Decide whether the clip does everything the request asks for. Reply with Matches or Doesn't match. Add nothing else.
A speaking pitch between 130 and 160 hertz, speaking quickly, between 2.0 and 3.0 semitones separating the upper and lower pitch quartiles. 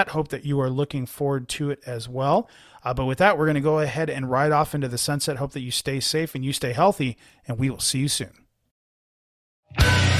Matches